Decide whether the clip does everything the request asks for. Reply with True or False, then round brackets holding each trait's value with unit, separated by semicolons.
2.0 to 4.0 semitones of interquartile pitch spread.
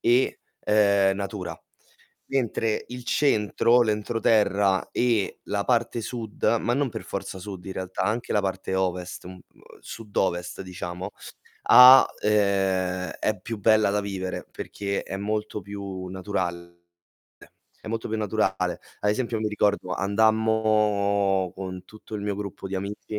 True (2.5 semitones)